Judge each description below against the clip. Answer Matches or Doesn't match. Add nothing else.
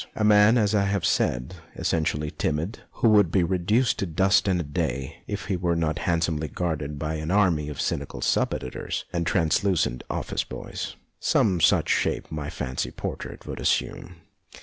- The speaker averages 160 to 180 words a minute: Matches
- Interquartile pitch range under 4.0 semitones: Doesn't match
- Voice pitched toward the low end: Matches